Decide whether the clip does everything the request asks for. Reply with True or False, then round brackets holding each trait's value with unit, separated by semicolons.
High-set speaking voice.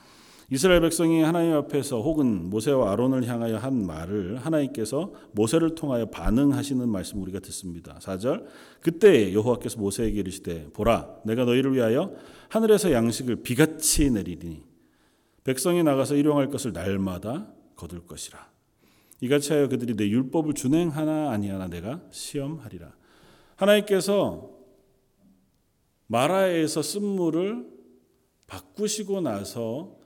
False (130 Hz)